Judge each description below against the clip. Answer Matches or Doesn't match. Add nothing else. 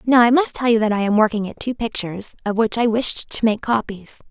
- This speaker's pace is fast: Matches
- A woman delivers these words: Matches